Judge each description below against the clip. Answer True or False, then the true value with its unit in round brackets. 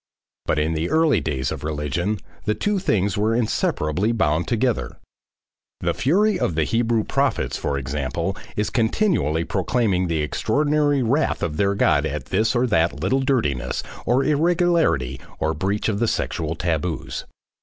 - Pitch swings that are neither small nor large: False (8.8 semitones)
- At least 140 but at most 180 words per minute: True (155 wpm)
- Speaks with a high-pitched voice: False (105 Hz)